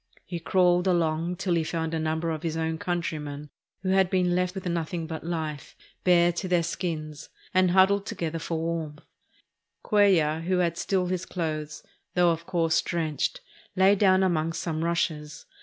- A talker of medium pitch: Yes, medium, 170 Hz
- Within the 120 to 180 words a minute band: Yes, average, 165 wpm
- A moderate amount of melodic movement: No, narrow, 2.3 semitones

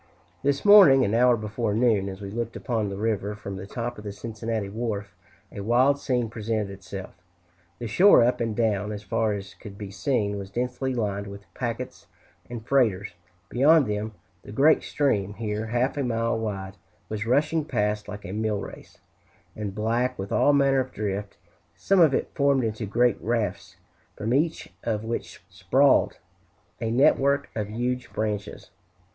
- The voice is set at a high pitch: No, low, 110 Hz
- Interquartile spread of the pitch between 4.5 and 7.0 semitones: No, average, 3.4 semitones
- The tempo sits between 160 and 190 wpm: Yes, average, 170 wpm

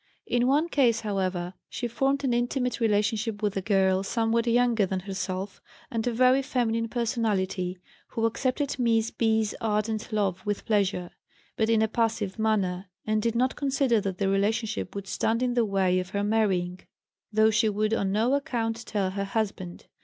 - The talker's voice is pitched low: No, high, 220 Hz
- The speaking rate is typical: Yes, average, 175 wpm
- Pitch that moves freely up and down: No, average, 3.1 semitones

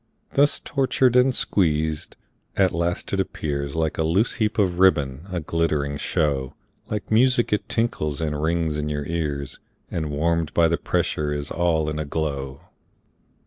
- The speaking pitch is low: Yes, very low, 80 Hz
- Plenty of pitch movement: No, average, 4.0 semitones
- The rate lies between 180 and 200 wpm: No, average, 160 wpm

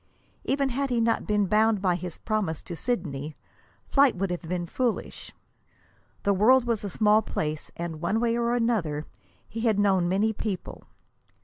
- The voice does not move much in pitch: No, average, 4.9 semitones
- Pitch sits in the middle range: No, high, 210 Hz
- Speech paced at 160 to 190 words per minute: Yes, average, 170 wpm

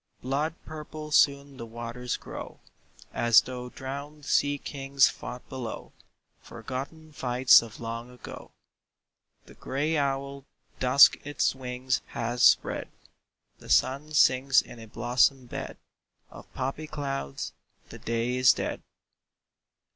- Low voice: Yes, low, 130 Hz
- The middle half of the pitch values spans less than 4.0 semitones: Yes, narrow, 2.4 semitones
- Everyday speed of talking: No, slow, 120 wpm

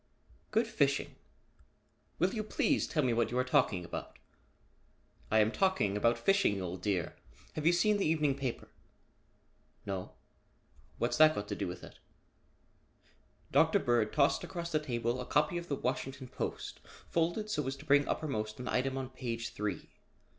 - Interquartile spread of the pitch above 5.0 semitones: Yes, wide, 5.4 semitones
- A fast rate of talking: No, average, 165 wpm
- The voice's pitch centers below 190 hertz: Yes, low, 135 Hz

